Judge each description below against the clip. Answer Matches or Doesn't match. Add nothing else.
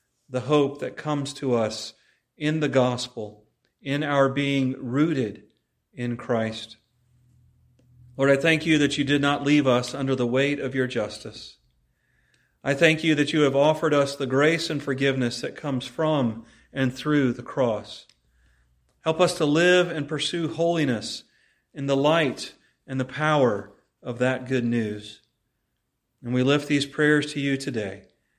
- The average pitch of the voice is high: Doesn't match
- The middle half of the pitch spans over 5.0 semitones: Doesn't match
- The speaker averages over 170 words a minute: Doesn't match